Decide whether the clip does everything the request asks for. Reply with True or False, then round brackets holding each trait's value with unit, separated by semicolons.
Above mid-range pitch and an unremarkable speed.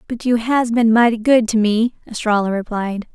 True (225 Hz; 190 wpm)